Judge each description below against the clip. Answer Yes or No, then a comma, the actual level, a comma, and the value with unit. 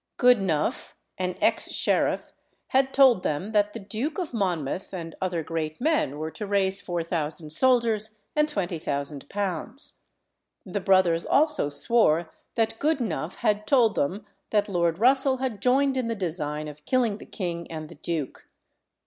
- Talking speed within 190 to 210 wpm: No, average, 150 wpm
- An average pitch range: No, wide, 6.4 semitones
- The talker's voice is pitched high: Yes, high, 195 Hz